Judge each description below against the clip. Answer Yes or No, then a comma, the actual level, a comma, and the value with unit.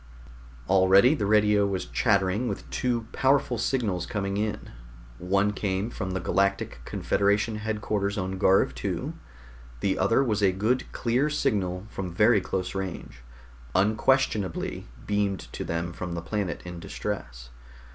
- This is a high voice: No, low, 100 Hz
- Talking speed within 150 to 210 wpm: No, slow, 135 wpm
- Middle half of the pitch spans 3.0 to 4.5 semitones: No, narrow, 2.6 semitones